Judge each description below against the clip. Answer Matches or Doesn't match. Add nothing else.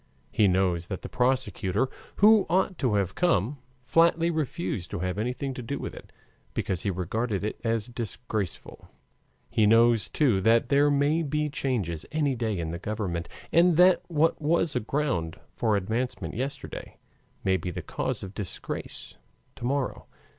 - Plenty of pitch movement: Matches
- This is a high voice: Doesn't match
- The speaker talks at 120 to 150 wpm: Doesn't match